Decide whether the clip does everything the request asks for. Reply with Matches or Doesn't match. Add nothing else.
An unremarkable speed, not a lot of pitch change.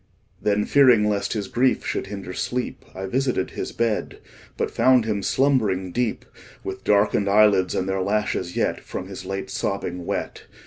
Doesn't match